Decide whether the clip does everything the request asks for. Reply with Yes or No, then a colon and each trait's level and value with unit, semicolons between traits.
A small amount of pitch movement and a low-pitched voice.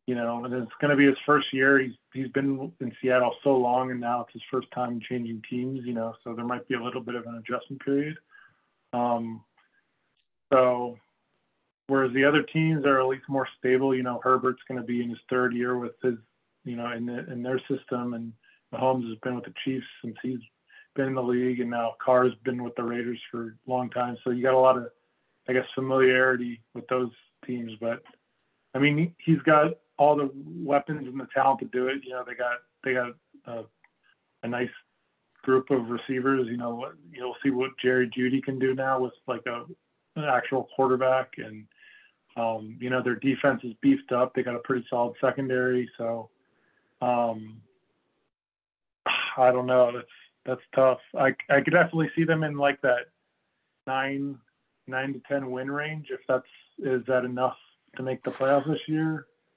Yes: narrow, 1.8 semitones; low, 130 Hz